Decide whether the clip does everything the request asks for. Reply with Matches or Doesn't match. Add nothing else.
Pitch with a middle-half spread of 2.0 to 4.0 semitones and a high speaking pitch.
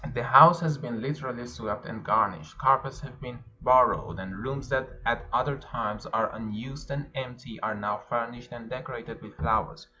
Doesn't match